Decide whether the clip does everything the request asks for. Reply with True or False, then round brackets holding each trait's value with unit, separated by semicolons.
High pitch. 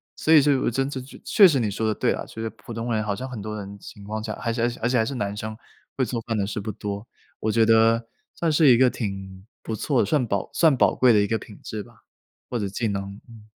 False (110 Hz)